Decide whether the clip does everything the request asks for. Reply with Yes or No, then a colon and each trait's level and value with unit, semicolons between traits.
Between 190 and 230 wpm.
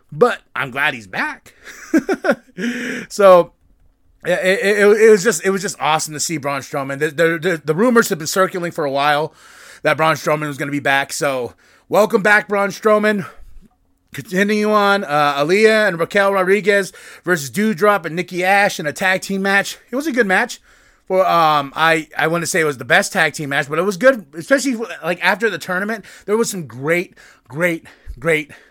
Yes: average, 195 wpm